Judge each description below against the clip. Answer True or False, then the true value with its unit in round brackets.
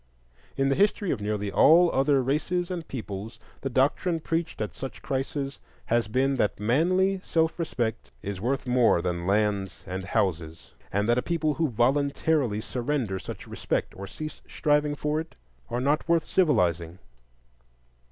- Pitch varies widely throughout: True (6.8 semitones)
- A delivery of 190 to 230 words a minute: False (155 wpm)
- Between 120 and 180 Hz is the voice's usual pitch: True (135 Hz)